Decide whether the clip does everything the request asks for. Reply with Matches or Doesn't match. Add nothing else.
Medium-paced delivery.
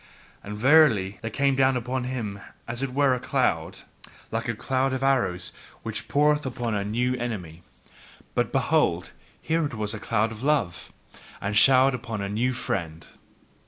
Matches